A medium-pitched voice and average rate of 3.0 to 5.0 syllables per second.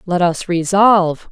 Yes: medium, 180 Hz; 4.2 syllables/s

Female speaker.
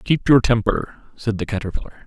No: male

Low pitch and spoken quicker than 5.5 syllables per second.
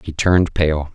No: very low, 80 Hz; 4.7 syllables/s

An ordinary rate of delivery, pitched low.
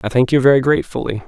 No: fast, 235 wpm; low, 130 Hz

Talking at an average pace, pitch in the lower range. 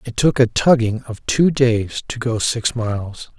Yes: average, 195 wpm; low, 115 Hz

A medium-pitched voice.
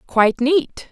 No: high, 235 Hz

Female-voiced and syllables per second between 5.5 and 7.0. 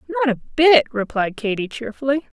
Yes: female; 5.6 syllables/s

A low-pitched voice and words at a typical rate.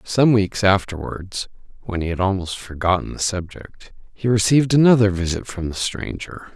Yes: low, 100 Hz; average, 155 wpm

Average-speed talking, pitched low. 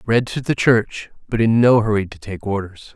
No: fast, 225 wpm; low, 110 Hz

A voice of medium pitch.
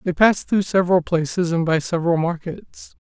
Yes: medium, 175 Hz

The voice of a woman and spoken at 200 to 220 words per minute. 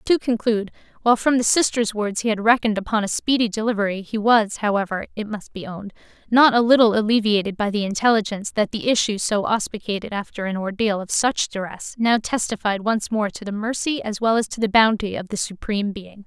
Yes: female; fast, 205 wpm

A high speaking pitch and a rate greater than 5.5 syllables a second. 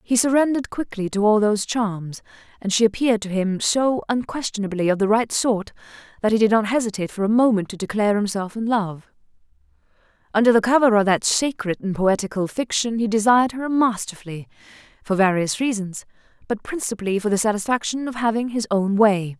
Yes: high, 215 Hz; 5.9 syllables/s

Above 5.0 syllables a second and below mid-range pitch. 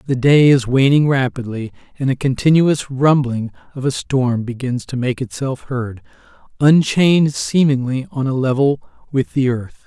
No: 4.6 syllables/s; low, 130 Hz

